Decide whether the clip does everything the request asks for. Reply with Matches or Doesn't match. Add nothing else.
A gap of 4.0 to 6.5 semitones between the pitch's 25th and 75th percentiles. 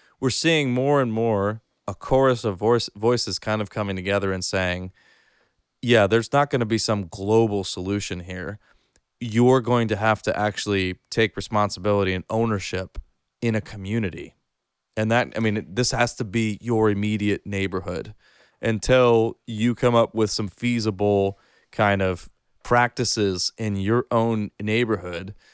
Doesn't match